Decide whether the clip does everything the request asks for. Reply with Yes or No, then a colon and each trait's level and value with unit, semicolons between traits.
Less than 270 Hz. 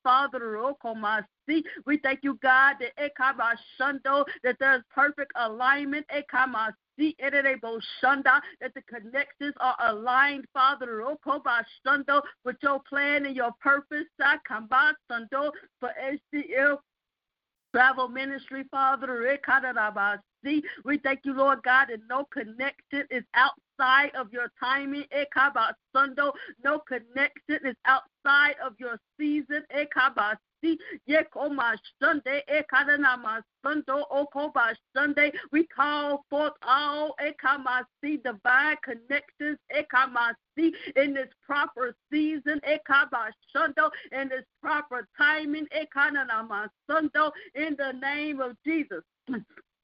No: very high, 275 Hz